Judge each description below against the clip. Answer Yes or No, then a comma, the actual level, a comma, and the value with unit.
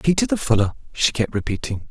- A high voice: No, low, 115 Hz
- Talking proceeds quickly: No, average, 190 wpm